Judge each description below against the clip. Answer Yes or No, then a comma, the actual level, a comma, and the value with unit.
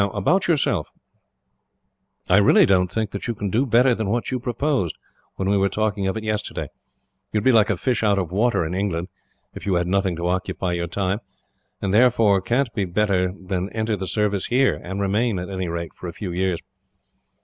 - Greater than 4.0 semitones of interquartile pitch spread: No, average, 3.4 semitones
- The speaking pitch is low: Yes, low, 100 Hz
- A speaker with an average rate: No, fast, 210 wpm